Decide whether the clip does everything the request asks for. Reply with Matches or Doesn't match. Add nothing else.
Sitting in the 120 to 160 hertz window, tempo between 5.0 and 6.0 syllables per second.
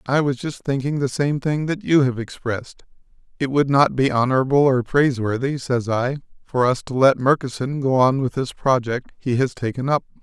Matches